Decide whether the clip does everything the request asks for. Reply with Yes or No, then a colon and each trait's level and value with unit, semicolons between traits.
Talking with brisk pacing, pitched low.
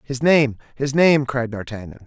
No: average, 175 wpm; low, 130 Hz